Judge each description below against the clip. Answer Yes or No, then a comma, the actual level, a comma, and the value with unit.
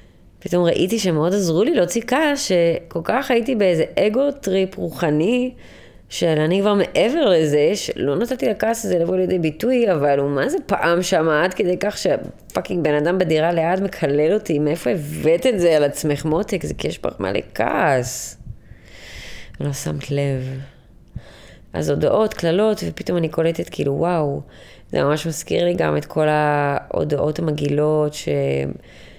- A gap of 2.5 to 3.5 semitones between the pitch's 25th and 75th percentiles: No, average, 4.3 semitones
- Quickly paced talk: Yes, fast, 155 wpm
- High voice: No, medium, 165 Hz